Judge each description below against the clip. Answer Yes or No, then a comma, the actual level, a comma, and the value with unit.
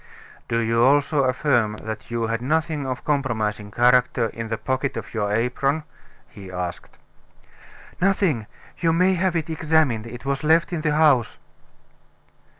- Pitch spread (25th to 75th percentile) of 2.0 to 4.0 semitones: No, average, 5.3 semitones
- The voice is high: No, low, 130 Hz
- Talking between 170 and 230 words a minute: No, average, 150 wpm